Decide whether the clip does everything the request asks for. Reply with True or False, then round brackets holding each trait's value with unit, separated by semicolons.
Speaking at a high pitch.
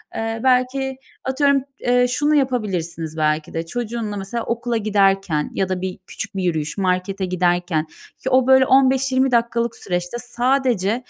True (225 Hz)